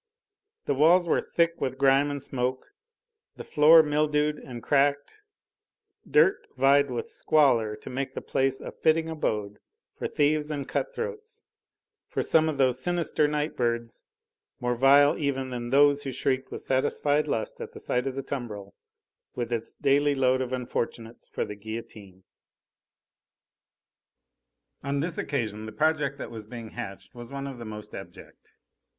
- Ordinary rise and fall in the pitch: Yes, average, 3.7 semitones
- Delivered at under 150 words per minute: No, average, 155 wpm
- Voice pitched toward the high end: No, low, 135 Hz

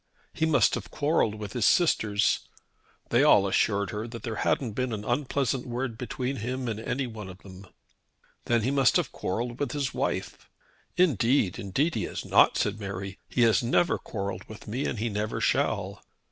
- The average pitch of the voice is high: No, low, 115 Hz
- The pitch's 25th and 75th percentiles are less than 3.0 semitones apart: No, average, 4.0 semitones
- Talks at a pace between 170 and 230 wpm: Yes, average, 185 wpm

